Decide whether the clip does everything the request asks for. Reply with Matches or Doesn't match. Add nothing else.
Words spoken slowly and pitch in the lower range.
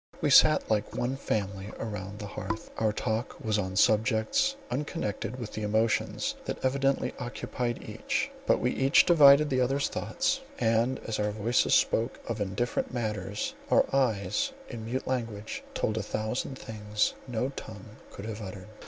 Doesn't match